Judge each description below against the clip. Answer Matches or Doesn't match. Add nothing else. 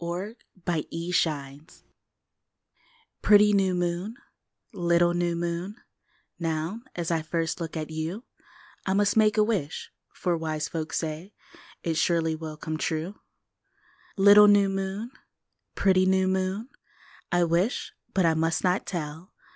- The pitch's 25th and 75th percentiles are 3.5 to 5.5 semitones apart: Doesn't match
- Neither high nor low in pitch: Matches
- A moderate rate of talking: Doesn't match